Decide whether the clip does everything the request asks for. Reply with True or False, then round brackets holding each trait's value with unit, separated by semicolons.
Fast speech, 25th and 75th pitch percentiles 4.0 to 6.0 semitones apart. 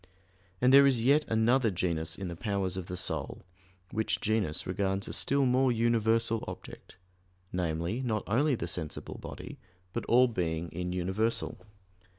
False (155 wpm; 4.9 semitones)